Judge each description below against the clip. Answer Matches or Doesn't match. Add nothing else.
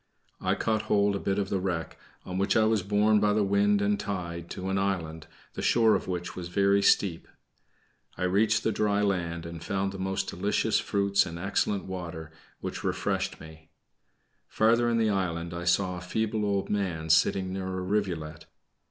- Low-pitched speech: Matches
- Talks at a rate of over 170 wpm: Matches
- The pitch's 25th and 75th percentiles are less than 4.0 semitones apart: Matches